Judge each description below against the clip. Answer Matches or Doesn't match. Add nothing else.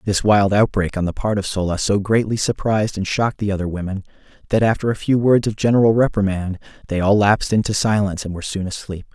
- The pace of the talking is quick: Matches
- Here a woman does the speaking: Doesn't match